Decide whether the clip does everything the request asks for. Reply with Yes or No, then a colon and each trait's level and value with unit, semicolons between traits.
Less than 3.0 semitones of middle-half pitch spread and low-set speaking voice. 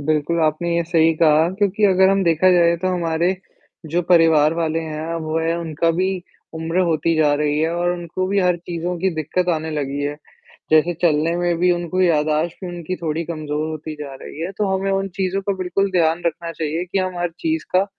No: narrow, 2.4 semitones; medium, 170 Hz